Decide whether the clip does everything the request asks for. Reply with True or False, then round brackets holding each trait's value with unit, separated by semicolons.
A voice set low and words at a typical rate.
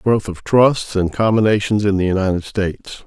True (100 Hz; 175 wpm)